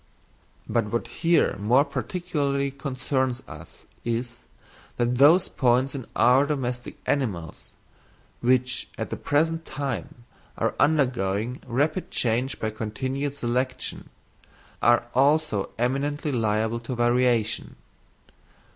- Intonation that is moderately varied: Yes, average, 3.0 semitones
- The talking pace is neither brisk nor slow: No, slow, 105 wpm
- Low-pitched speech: Yes, low, 125 Hz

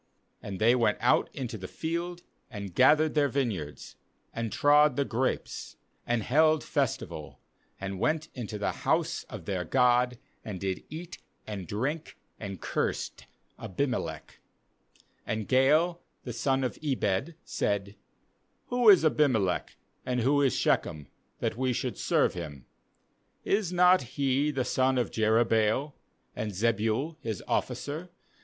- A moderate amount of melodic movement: No, wide, 5.9 semitones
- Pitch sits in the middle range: No, low, 125 Hz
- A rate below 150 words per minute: Yes, slow, 135 wpm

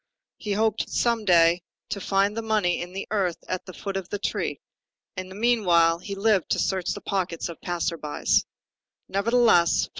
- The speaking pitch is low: No, high, 195 Hz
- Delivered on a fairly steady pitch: No, average, 3.2 semitones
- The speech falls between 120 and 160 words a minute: No, average, 175 wpm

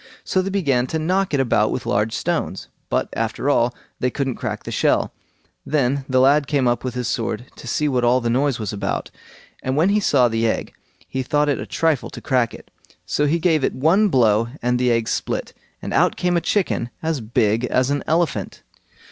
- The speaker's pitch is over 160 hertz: No, low, 130 Hz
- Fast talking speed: Yes, fast, 215 wpm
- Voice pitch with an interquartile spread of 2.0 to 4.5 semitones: Yes, average, 4.1 semitones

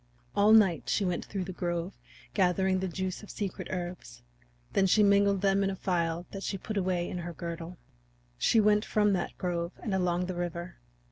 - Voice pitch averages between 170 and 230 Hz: Yes, medium, 185 Hz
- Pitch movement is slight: Yes, narrow, 2.3 semitones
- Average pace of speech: Yes, average, 195 wpm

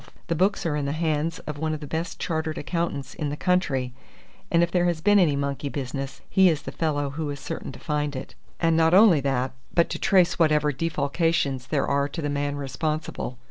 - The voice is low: No, medium, 150 Hz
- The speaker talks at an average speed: No, fast, 220 wpm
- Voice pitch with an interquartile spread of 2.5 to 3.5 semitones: Yes, average, 2.9 semitones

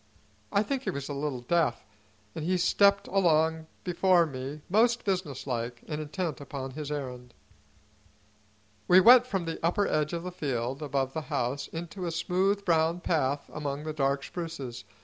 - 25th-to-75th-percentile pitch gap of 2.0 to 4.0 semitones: No, average, 4.5 semitones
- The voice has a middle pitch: Yes, medium, 155 Hz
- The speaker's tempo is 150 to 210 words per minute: Yes, average, 165 wpm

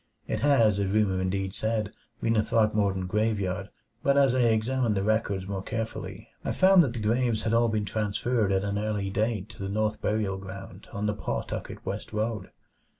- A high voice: No, low, 105 Hz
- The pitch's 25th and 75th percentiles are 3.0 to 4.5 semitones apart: No, narrow, 2.6 semitones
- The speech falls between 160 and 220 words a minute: Yes, average, 190 wpm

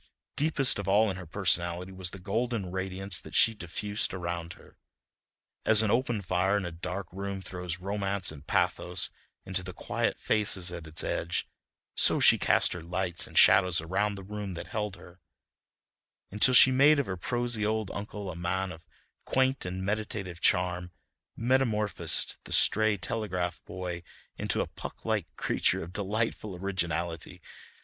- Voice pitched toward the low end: Yes, very low, 95 Hz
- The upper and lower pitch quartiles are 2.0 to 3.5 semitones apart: Yes, average, 3.0 semitones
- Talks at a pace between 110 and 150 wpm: No, average, 160 wpm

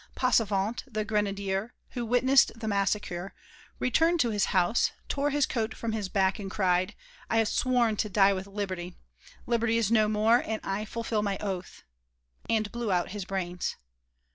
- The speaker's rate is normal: Yes, average, 165 wpm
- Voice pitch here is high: Yes, high, 210 Hz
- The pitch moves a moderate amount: Yes, average, 3.1 semitones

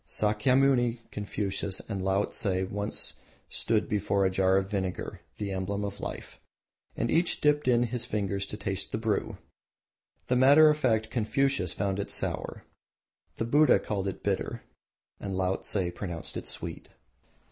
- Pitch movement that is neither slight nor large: Yes, average, 3.7 semitones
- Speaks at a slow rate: No, average, 145 wpm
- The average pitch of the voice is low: Yes, low, 105 Hz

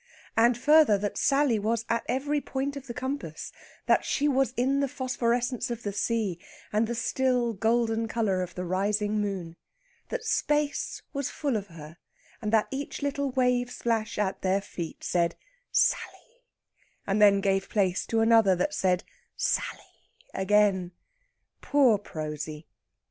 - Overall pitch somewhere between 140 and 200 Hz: No, high, 225 Hz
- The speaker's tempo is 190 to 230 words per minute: No, average, 150 wpm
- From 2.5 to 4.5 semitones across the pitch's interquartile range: No, average, 5.1 semitones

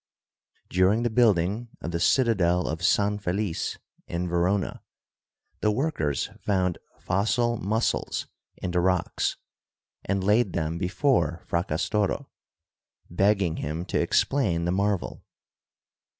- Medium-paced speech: No, slow, 115 wpm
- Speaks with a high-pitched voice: No, very low, 95 Hz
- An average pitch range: Yes, average, 3.4 semitones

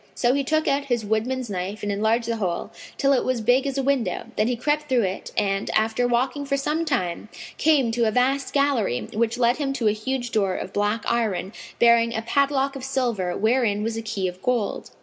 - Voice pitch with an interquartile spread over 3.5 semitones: Yes, average, 4.0 semitones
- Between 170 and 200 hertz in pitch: No, high, 235 Hz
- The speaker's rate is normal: No, fast, 220 wpm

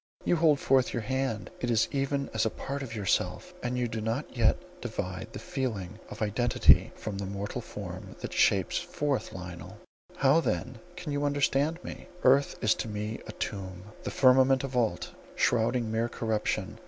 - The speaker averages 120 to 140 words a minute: No, average, 180 wpm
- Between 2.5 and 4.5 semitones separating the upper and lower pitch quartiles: Yes, average, 4.1 semitones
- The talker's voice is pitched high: No, low, 120 Hz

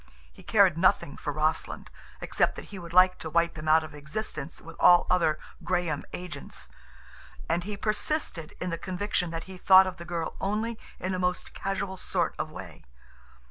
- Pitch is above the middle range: No, medium, 180 Hz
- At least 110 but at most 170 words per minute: No, average, 180 wpm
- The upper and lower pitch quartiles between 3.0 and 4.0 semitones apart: No, narrow, 2.5 semitones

